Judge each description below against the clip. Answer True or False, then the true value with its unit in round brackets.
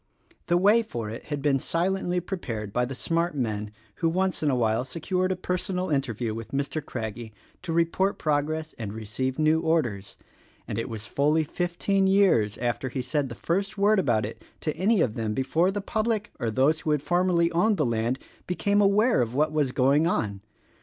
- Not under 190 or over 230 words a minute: True (195 wpm)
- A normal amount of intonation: False (7.1 semitones)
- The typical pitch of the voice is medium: True (155 Hz)